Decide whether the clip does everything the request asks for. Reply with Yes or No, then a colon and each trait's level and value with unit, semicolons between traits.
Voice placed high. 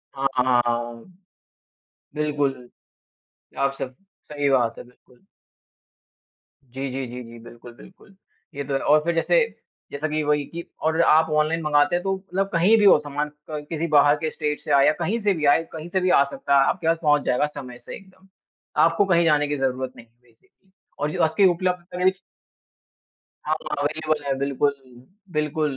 No: medium, 150 Hz